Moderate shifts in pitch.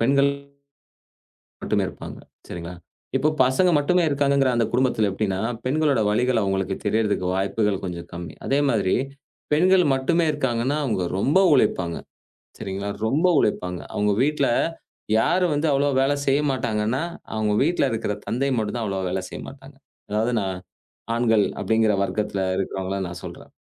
No: wide, 5.9 semitones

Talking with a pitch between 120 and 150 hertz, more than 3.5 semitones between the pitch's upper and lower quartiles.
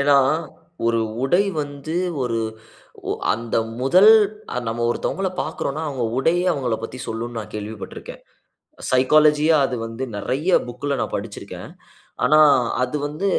Yes: low, 135 Hz; average, 4.5 semitones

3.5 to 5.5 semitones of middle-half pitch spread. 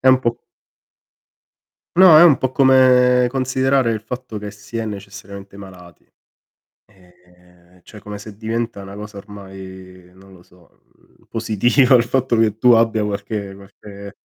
Yes: average, 4.0 semitones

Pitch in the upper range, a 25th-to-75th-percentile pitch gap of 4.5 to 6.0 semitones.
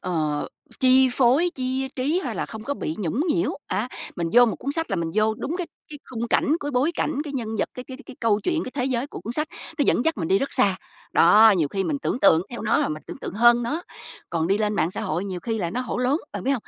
Yes: high, 240 Hz; wide, 5.5 semitones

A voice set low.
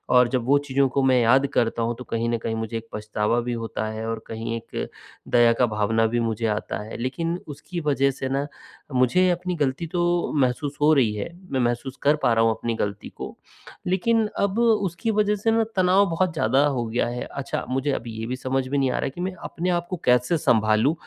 Yes: low, 130 Hz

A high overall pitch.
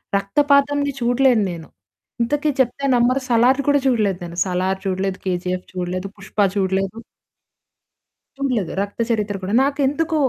Yes: high, 215 Hz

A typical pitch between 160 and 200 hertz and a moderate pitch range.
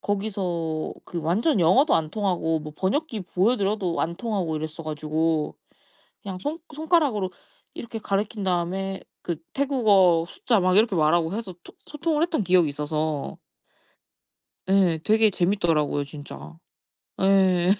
Yes: medium, 185 Hz; average, 4.7 semitones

